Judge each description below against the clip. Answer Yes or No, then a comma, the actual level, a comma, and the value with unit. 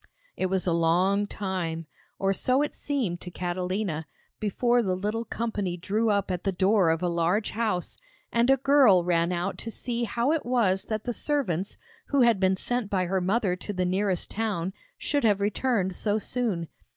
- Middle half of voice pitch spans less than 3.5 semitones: No, average, 4.2 semitones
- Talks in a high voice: Yes, high, 200 Hz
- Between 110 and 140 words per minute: No, average, 190 wpm